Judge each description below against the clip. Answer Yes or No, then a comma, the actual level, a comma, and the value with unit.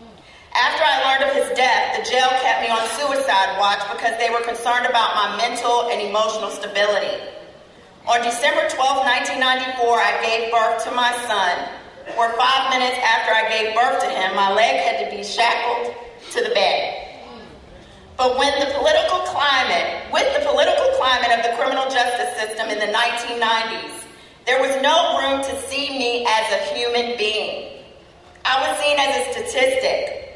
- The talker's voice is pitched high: Yes, high, 245 Hz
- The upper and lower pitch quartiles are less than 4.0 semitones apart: Yes, average, 3.2 semitones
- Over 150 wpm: Yes, average, 170 wpm